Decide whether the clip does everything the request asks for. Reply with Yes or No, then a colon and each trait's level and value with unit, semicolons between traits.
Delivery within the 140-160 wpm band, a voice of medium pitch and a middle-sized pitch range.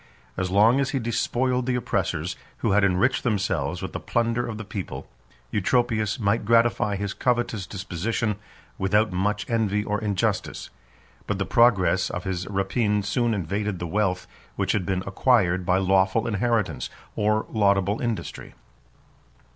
No: average, 150 wpm; low, 105 Hz; average, 3.4 semitones